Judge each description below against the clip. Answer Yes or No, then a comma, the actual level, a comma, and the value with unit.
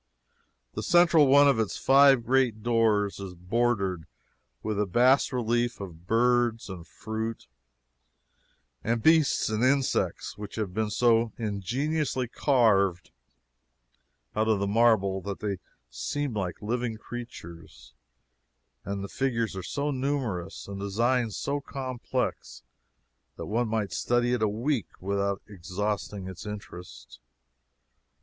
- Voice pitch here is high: No, low, 110 Hz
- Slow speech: Yes, slow, 130 wpm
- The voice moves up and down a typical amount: Yes, average, 3.8 semitones